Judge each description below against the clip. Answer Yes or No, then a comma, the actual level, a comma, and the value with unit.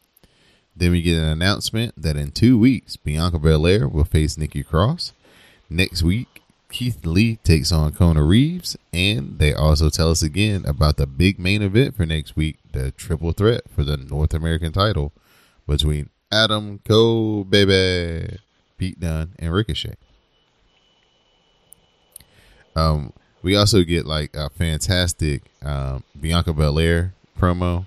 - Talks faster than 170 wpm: No, average, 140 wpm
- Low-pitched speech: Yes, very low, 85 Hz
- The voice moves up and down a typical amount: Yes, average, 4.4 semitones